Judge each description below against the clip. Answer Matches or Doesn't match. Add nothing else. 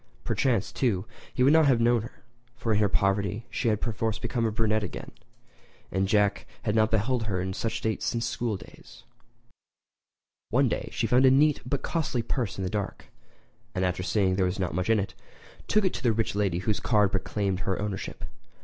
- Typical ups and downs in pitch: Matches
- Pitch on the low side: Matches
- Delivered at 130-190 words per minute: Doesn't match